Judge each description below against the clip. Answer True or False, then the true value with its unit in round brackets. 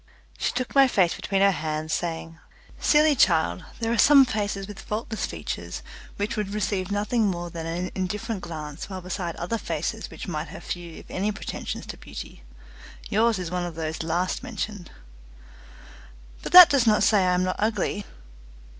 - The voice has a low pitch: False (195 Hz)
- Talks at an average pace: True (175 wpm)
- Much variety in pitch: False (3.9 semitones)